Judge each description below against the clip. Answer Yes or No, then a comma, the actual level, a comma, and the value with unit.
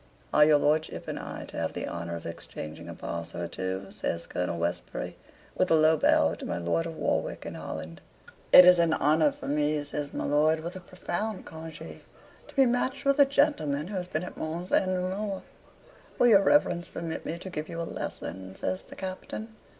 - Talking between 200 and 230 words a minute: Yes, fast, 205 wpm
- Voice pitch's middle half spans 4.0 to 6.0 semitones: Yes, average, 4.5 semitones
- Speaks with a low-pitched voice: No, medium, 160 Hz